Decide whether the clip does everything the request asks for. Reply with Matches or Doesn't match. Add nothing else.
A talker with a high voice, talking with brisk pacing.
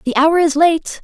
Matches